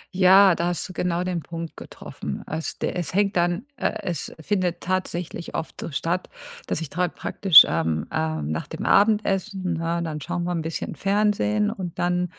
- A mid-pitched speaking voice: Yes, medium, 175 Hz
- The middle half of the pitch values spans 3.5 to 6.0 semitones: No, narrow, 2.6 semitones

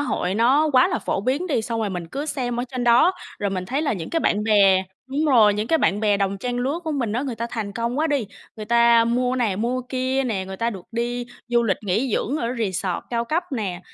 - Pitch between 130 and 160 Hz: No, high, 235 Hz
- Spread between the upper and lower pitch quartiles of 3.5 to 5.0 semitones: Yes, average, 3.9 semitones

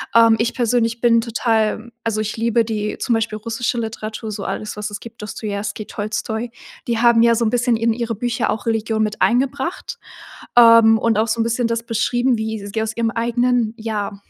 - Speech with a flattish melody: Yes, narrow, 1.3 semitones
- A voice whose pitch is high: Yes, high, 225 Hz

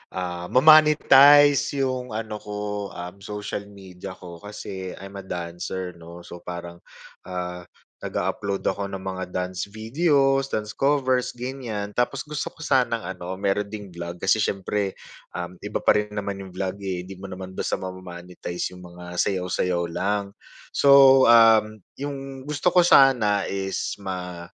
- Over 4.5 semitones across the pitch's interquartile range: Yes, average, 5.2 semitones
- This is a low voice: Yes, low, 100 Hz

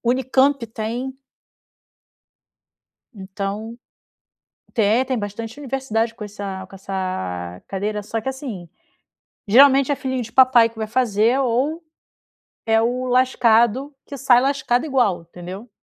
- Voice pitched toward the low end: No, high, 230 Hz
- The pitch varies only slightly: No, average, 4.1 semitones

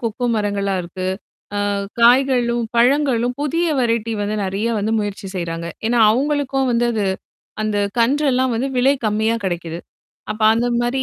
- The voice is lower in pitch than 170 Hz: No, high, 230 Hz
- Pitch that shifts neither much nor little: Yes, average, 3.8 semitones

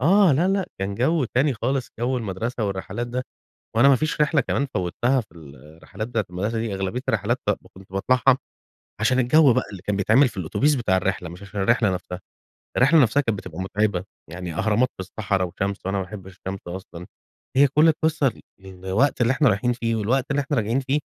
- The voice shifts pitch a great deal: Yes, wide, 5.7 semitones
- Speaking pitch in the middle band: No, low, 115 Hz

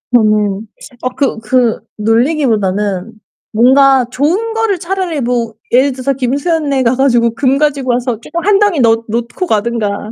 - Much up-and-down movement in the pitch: No, average, 4.2 semitones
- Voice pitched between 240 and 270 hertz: Yes, very high, 250 Hz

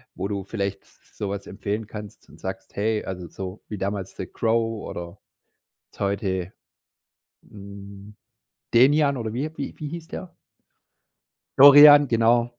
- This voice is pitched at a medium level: No, low, 105 Hz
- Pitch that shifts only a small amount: No, average, 3.5 semitones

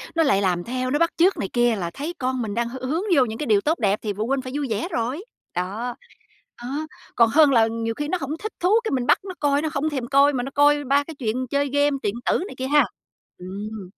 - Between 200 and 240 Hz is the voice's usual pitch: No, very high, 255 Hz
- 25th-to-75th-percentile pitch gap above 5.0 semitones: No, average, 4.6 semitones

